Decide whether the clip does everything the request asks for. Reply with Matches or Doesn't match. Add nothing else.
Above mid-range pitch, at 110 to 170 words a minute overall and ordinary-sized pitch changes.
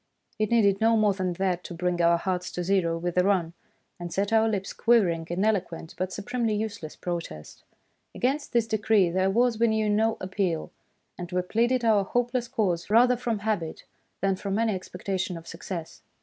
Doesn't match